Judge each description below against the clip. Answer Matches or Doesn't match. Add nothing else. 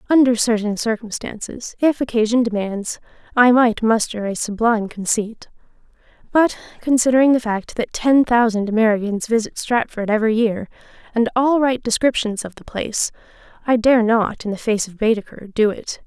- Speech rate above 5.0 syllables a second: Matches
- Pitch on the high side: Matches